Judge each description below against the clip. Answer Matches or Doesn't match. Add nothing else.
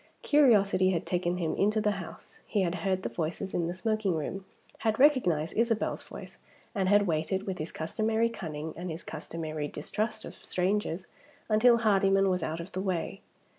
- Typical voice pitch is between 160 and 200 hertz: Matches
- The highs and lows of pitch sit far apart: Doesn't match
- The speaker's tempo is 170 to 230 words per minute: Matches